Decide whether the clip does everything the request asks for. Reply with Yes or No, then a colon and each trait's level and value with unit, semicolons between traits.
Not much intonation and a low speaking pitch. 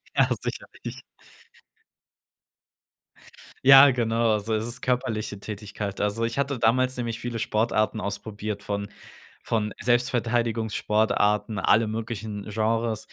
Yes: narrow, 1.9 semitones; low, 110 Hz